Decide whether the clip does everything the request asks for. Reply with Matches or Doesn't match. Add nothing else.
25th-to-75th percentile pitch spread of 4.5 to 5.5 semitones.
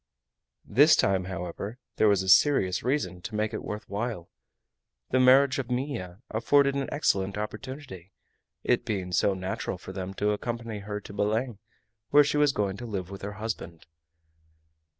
Matches